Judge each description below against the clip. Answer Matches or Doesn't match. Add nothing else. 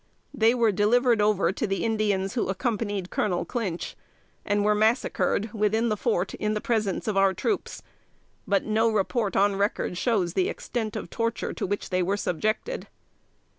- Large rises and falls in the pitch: Doesn't match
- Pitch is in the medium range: Doesn't match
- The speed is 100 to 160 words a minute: Doesn't match